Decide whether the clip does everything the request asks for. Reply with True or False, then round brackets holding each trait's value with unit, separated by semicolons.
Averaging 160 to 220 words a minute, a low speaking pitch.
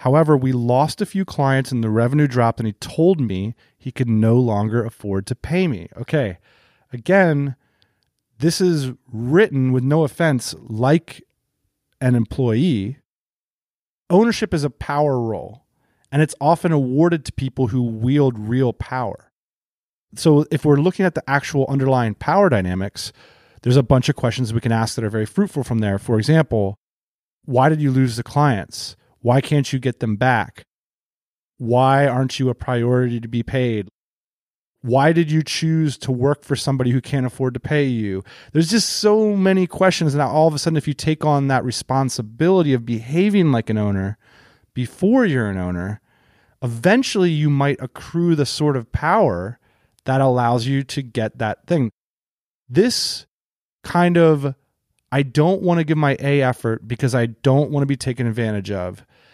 True (170 wpm; 130 Hz)